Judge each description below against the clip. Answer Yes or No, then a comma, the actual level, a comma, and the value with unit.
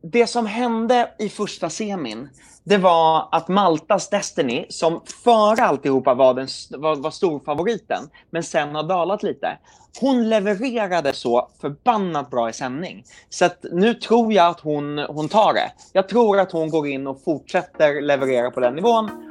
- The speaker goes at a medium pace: Yes, average, 160 wpm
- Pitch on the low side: No, medium, 175 Hz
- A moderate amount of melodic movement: No, wide, 7.0 semitones